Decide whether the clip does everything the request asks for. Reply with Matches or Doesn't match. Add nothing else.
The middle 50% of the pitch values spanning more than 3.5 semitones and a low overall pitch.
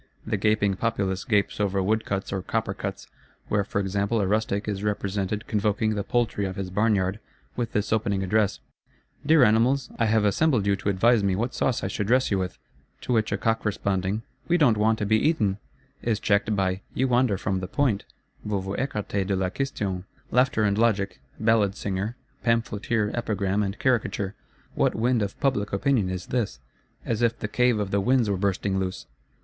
Doesn't match